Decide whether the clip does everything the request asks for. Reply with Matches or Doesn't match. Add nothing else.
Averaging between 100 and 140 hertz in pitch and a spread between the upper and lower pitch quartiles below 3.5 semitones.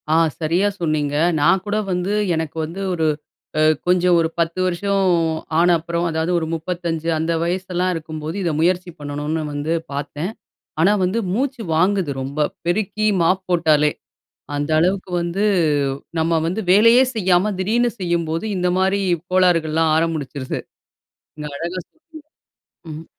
Doesn't match